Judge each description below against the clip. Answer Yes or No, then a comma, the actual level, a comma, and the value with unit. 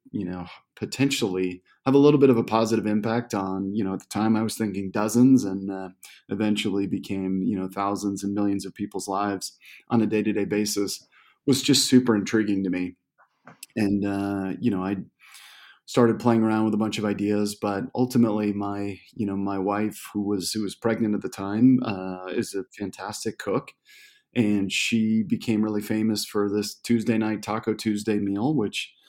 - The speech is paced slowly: No, average, 185 wpm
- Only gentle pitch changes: Yes, narrow, 2.2 semitones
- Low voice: Yes, low, 105 Hz